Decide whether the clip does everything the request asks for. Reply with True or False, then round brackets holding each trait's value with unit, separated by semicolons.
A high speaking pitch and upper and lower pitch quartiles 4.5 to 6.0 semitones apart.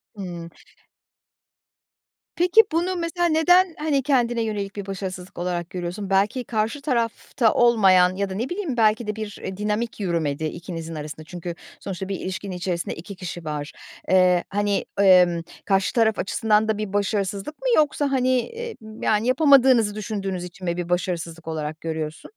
True (200 Hz; 5.0 semitones)